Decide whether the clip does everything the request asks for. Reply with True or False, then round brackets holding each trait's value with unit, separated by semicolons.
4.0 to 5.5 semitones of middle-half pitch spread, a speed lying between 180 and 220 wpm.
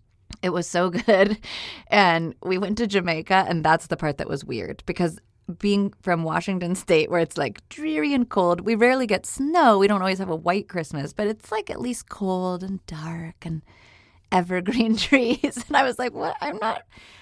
True (4.3 semitones; 200 wpm)